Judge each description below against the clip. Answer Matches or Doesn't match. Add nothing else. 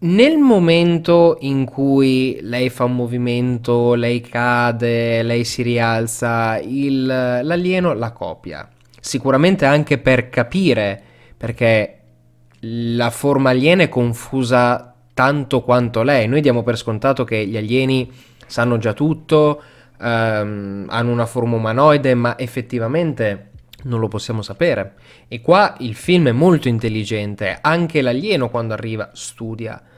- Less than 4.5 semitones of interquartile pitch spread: Matches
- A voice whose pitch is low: Matches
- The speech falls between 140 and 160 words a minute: Doesn't match